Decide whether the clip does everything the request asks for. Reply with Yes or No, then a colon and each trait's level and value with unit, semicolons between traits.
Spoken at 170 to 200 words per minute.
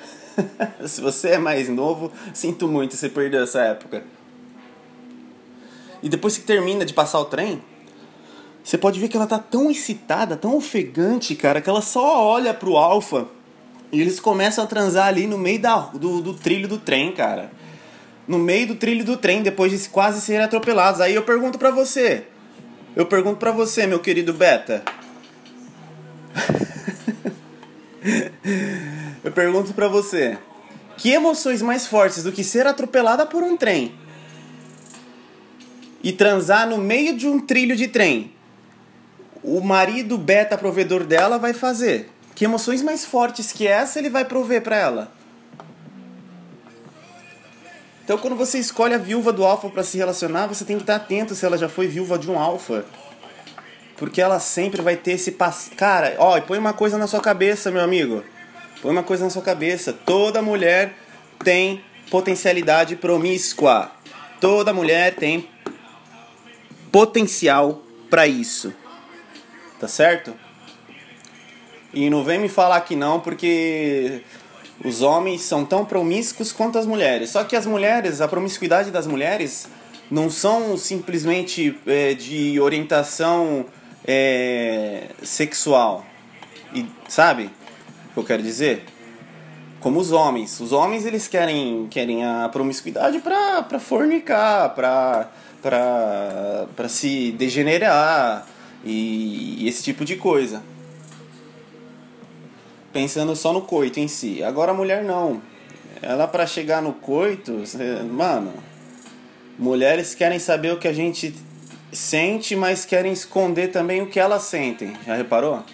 No: average, 140 wpm